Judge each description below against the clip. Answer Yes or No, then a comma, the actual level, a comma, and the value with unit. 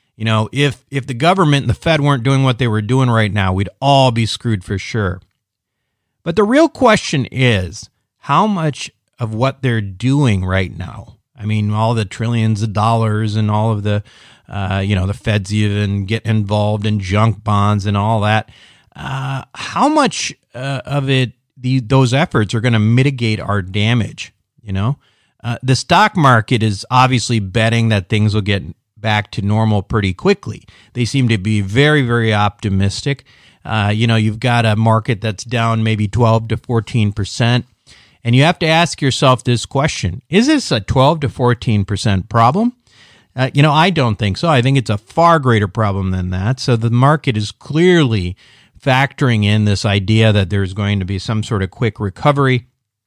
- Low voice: Yes, low, 115 Hz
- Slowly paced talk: No, average, 185 wpm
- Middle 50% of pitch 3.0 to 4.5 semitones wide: Yes, average, 4.1 semitones